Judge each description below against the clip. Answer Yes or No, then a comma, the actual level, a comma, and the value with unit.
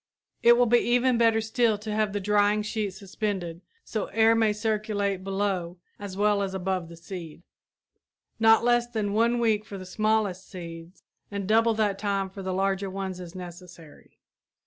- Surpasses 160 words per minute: Yes, average, 170 wpm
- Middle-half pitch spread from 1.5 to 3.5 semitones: Yes, average, 2.8 semitones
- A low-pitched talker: No, high, 205 Hz